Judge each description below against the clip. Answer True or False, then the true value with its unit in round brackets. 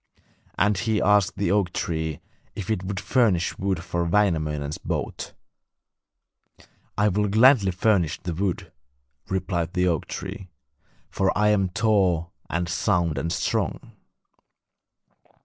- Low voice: True (95 Hz)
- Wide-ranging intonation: False (3.3 semitones)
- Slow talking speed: True (125 wpm)